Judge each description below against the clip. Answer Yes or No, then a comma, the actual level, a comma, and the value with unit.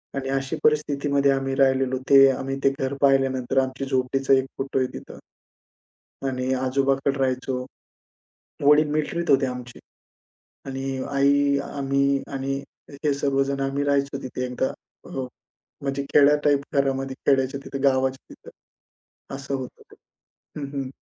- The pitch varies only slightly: Yes, narrow, 0.9 semitones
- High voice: No, low, 135 Hz